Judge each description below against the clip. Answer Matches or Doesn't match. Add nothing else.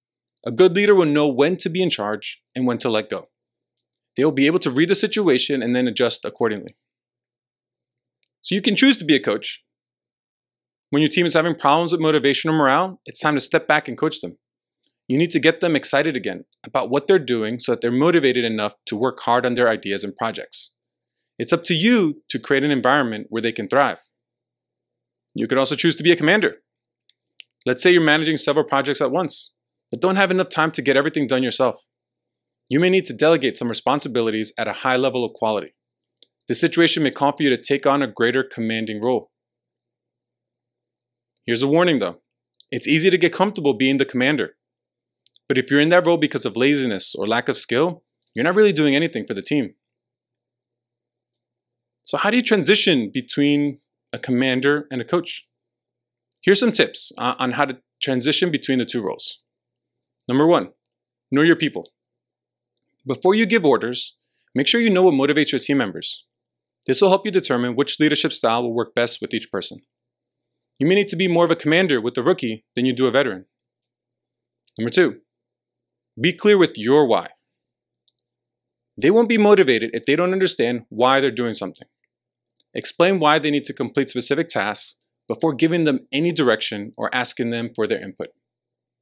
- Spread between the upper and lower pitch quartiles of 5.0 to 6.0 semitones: Matches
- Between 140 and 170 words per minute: Doesn't match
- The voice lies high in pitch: Doesn't match